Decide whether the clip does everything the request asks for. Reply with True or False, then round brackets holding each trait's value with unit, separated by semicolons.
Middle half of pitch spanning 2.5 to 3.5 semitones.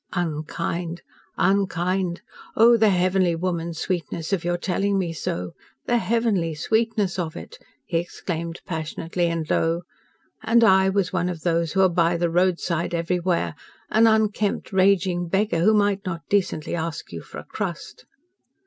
True (2.8 semitones)